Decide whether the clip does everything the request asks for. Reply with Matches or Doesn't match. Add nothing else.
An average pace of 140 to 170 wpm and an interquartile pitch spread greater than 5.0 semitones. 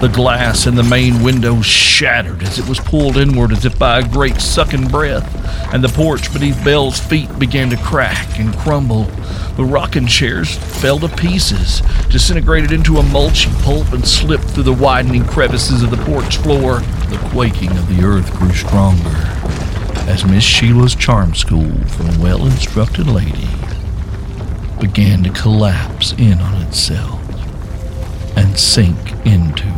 Matches